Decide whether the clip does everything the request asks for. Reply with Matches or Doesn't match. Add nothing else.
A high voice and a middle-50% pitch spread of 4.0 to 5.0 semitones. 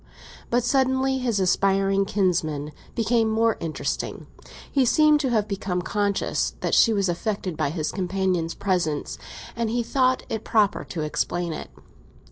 Matches